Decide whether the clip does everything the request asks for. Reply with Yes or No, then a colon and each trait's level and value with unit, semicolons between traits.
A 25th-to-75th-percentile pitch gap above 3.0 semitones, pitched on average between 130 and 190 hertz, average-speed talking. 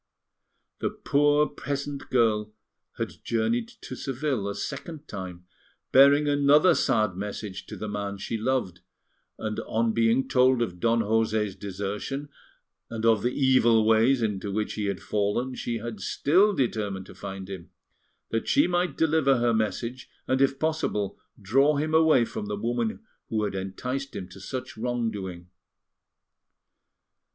No: average, 4.8 semitones; low, 115 Hz; average, 150 wpm